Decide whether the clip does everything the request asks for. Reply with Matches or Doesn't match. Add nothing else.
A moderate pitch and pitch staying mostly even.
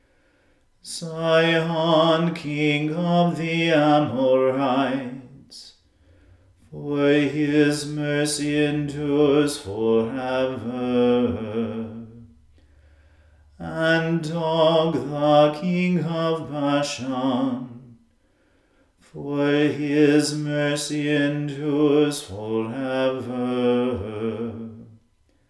Doesn't match